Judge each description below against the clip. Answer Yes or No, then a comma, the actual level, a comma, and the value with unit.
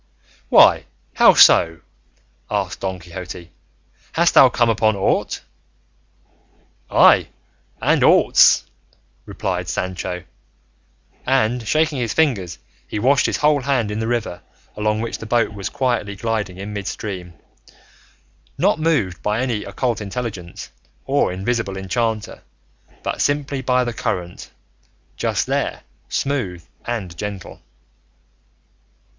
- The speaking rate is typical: No, slow, 115 wpm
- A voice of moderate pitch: No, low, 110 Hz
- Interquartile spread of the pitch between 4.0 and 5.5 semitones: Yes, average, 4.6 semitones